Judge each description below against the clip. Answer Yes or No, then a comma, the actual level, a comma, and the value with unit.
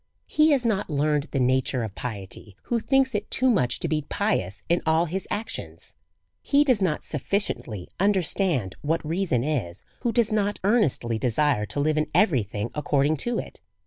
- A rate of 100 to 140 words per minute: No, average, 180 wpm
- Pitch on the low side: No, medium, 155 Hz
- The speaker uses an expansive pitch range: Yes, wide, 8.6 semitones